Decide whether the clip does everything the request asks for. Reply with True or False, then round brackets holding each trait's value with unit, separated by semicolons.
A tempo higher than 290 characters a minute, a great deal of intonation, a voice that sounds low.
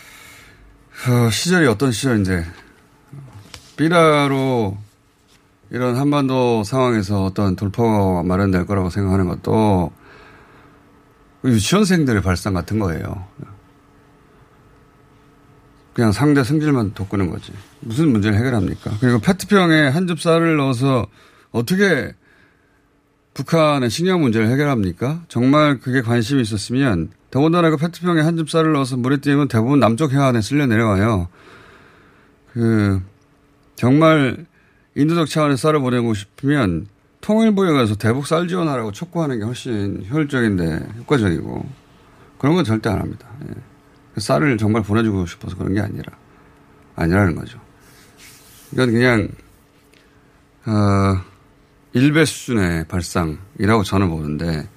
False (275 characters per minute; 6.1 semitones; 120 Hz)